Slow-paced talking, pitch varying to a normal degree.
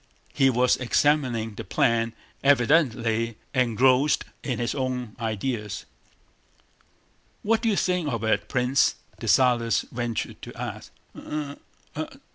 Yes: slow, 115 wpm; average, 3.3 semitones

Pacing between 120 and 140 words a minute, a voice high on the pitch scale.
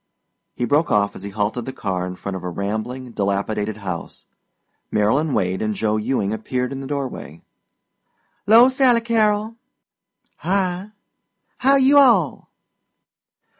No: slow, 135 wpm; low, 125 Hz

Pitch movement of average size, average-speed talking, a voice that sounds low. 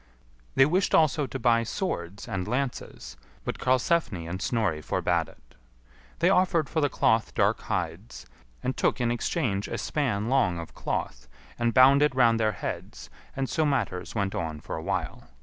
No: wide, 6.3 semitones; average, 170 wpm; low, 120 Hz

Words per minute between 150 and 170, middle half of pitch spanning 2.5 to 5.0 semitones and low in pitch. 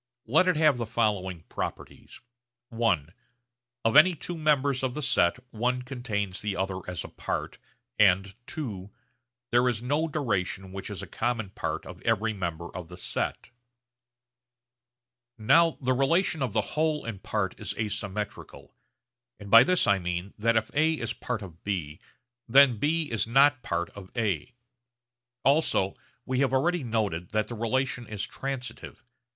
No: average, 155 wpm; wide, 5.6 semitones; low, 115 Hz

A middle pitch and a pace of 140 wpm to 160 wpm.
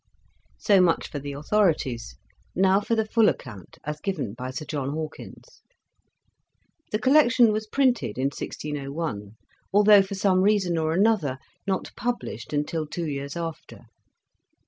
Yes: medium, 165 Hz; average, 145 wpm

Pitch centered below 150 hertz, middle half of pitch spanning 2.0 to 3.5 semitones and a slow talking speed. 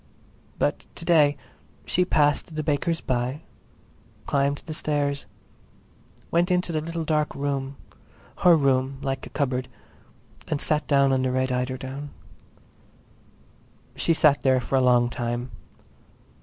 Yes: medium, 140 Hz; average, 2.9 semitones; slow, 125 wpm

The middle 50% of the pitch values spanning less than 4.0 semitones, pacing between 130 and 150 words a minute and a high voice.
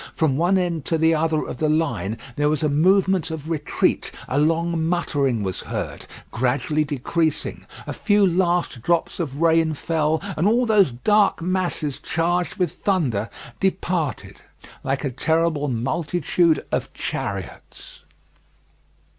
No: average, 3.3 semitones; average, 140 wpm; medium, 160 Hz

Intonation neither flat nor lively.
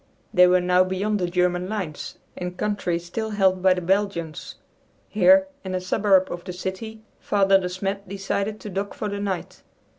No: narrow, 2.0 semitones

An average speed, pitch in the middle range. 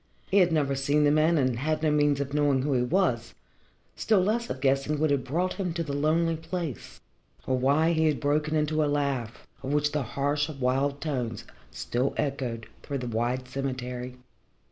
Yes: average, 190 wpm; medium, 145 Hz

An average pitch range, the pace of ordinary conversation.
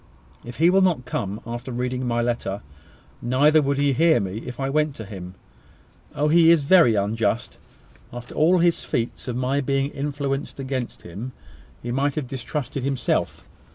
Yes: average, 3.5 semitones; average, 170 wpm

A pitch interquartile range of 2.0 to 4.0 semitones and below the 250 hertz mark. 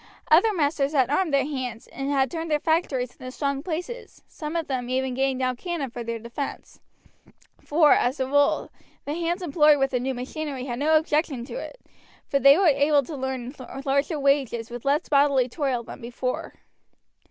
No: average, 3.1 semitones; very high, 275 Hz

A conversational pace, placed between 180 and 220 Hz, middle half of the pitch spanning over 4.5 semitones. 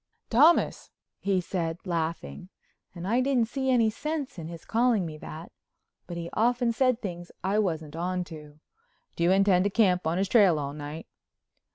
Yes: average, 175 wpm; medium, 185 Hz; wide, 5.6 semitones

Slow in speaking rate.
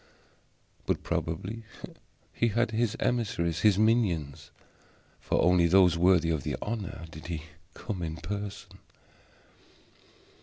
Yes: slow, 115 wpm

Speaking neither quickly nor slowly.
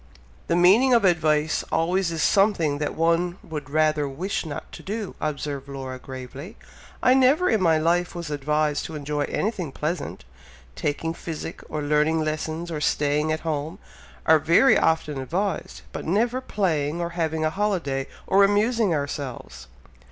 Yes: average, 155 wpm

